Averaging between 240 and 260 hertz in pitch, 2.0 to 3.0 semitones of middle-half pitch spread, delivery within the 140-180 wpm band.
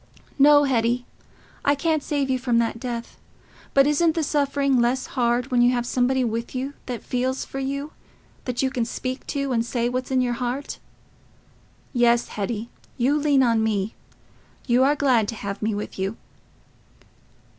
Yes: very high, 250 Hz; average, 2.7 semitones; average, 165 wpm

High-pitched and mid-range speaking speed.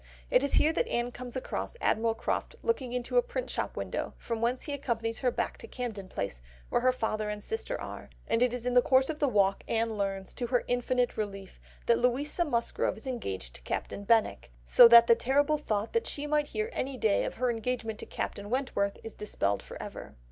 No: high, 240 Hz; fast, 215 wpm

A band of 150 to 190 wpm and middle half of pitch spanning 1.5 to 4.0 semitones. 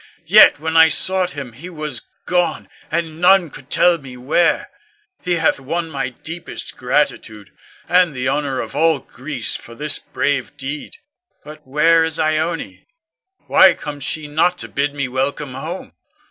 Yes: average, 160 wpm; average, 3.4 semitones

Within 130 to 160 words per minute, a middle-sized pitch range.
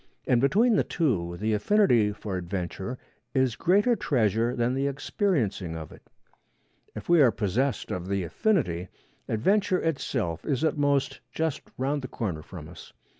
No: average, 155 wpm; wide, 7.6 semitones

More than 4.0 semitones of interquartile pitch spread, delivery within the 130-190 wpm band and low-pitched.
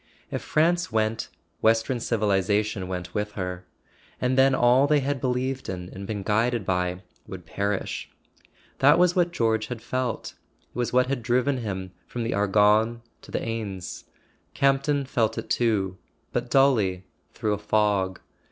Yes: average, 4.4 semitones; average, 155 wpm; low, 110 Hz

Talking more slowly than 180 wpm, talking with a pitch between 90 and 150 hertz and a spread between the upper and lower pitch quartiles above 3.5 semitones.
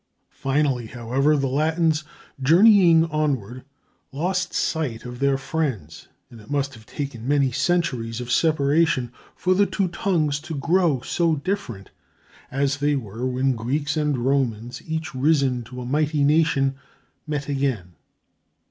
Yes: average, 140 wpm; medium, 140 Hz; average, 3.9 semitones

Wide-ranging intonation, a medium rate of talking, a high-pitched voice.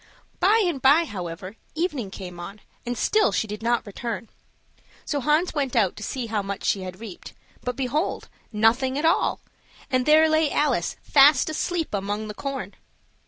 Yes: wide, 6.4 semitones; average, 170 wpm; very high, 250 Hz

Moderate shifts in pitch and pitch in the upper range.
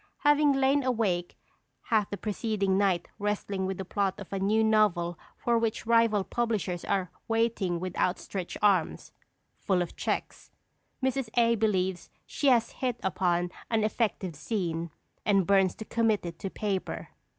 Yes: average, 3.6 semitones; high, 205 Hz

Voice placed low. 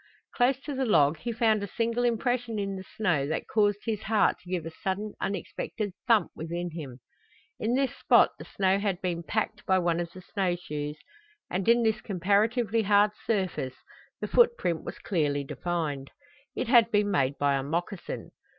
No: high, 195 Hz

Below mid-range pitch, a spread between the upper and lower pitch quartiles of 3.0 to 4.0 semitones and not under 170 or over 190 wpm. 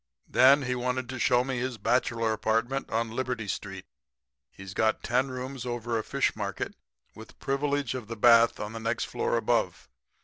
No: low, 120 Hz; narrow, 2.5 semitones; average, 175 wpm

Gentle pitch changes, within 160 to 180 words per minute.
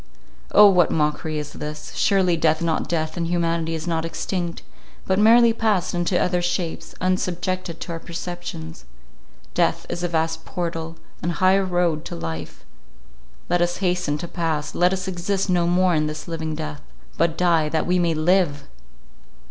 Yes: narrow, 2.1 semitones; average, 170 wpm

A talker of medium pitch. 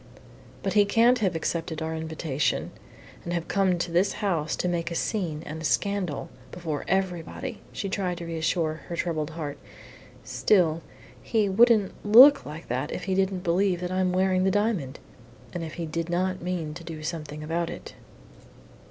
Yes: medium, 175 Hz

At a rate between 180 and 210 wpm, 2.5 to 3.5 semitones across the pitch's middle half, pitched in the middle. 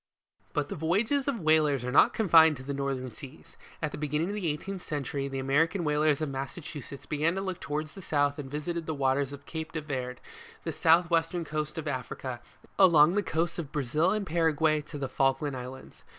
Yes: fast, 205 wpm; average, 3.1 semitones; medium, 150 Hz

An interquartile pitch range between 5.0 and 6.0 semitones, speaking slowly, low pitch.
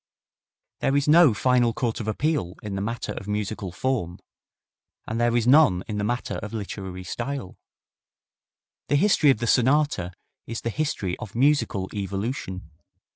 No: average, 5.3 semitones; average, 155 wpm; low, 115 Hz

